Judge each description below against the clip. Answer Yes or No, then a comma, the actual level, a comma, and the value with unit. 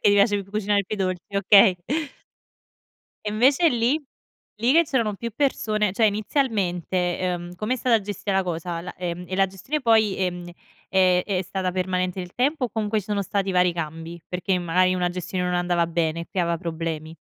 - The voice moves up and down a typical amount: Yes, average, 3.2 semitones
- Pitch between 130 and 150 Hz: No, high, 190 Hz